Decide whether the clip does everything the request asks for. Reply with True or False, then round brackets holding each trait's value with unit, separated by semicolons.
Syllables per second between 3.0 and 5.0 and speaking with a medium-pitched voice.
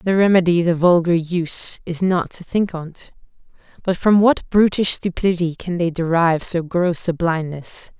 True (4.7 syllables/s; 175 Hz)